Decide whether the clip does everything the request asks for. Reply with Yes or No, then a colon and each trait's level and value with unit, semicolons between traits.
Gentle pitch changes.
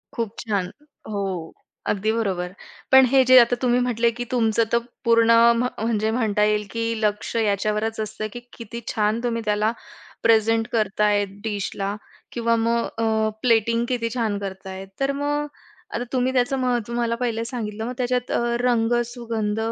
Yes: narrow, 2.3 semitones